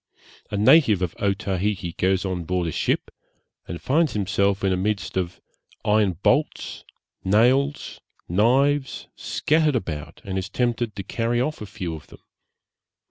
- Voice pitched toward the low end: Yes, low, 100 Hz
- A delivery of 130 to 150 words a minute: Yes, average, 145 wpm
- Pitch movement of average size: Yes, average, 4.6 semitones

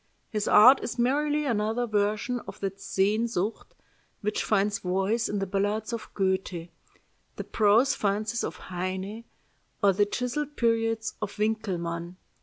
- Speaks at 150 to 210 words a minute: No, slow, 135 wpm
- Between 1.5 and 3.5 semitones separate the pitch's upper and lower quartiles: Yes, average, 3.0 semitones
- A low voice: No, high, 210 Hz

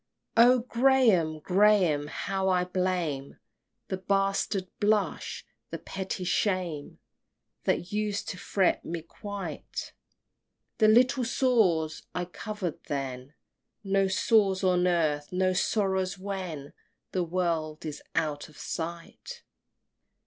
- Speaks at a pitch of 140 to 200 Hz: Yes, medium, 185 Hz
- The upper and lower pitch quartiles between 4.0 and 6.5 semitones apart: No, average, 3.6 semitones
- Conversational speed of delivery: No, slow, 110 wpm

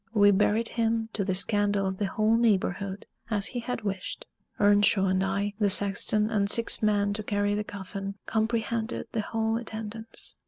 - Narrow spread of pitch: Yes, narrow, 1.9 semitones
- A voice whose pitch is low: No, high, 205 Hz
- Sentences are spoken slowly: No, average, 170 wpm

